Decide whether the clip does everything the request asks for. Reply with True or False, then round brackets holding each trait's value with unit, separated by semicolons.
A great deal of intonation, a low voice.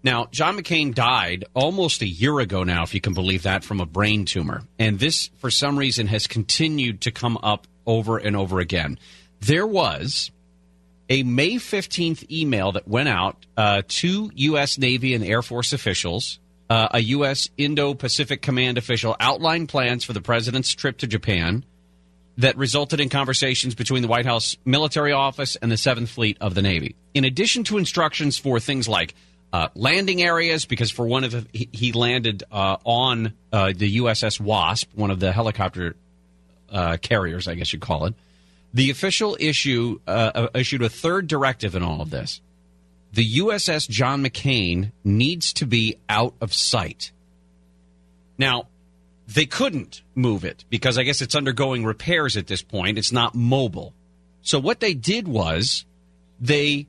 True (6.6 semitones; 115 Hz)